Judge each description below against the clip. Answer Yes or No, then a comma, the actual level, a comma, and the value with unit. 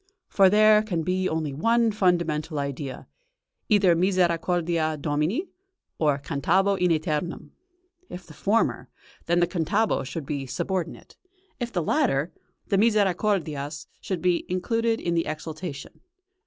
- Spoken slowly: Yes, slow, 130 wpm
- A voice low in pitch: No, medium, 175 Hz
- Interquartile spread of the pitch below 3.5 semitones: No, average, 4.2 semitones